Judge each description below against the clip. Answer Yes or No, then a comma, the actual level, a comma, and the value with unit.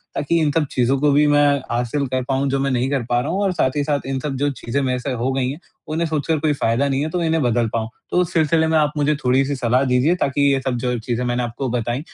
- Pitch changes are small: No, average, 3.0 semitones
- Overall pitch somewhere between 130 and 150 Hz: Yes, low, 135 Hz